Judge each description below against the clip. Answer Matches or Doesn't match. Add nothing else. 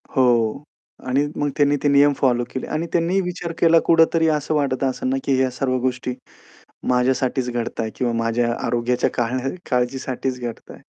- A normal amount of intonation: Matches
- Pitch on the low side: Matches